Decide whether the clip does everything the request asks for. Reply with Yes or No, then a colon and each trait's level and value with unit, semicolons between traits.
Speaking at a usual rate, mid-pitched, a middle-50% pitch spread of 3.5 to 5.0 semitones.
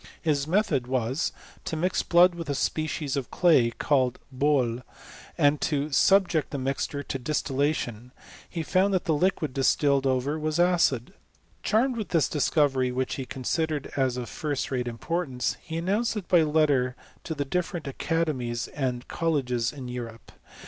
Yes: average, 165 wpm; medium, 145 Hz; average, 4.3 semitones